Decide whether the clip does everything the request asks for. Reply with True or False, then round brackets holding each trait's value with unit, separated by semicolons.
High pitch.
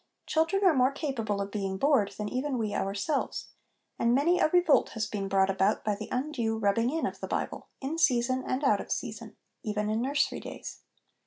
True (240 Hz)